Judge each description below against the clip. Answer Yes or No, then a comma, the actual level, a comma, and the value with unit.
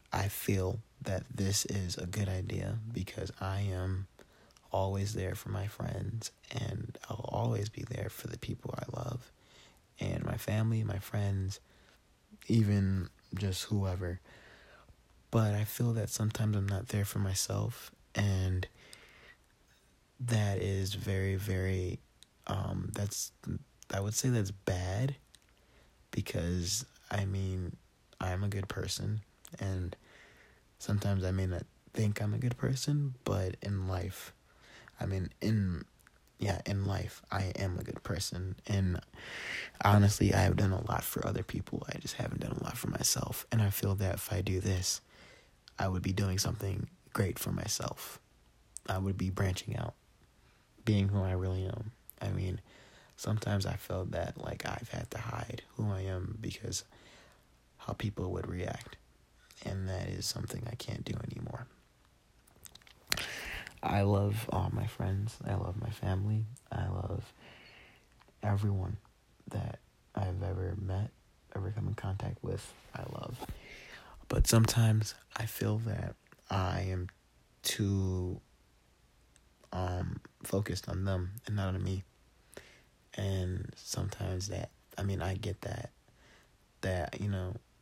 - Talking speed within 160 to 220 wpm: No, average, 145 wpm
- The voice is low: Yes, low, 100 Hz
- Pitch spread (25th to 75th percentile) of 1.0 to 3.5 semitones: Yes, average, 2.9 semitones